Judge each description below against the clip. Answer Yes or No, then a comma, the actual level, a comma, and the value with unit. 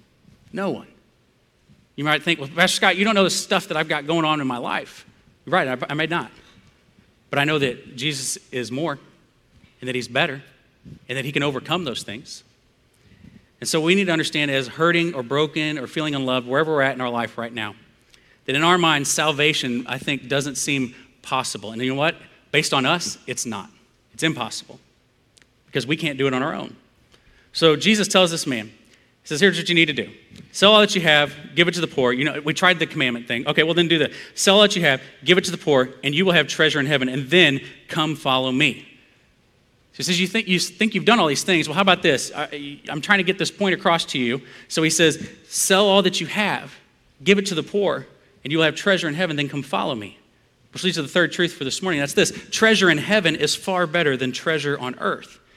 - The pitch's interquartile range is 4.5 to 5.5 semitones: Yes, average, 5.0 semitones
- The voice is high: No, medium, 155 Hz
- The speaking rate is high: Yes, fast, 240 wpm